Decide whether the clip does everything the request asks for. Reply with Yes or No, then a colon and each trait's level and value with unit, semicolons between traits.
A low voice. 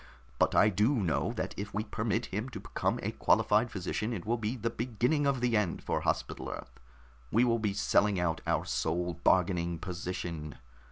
Yes: low, 105 Hz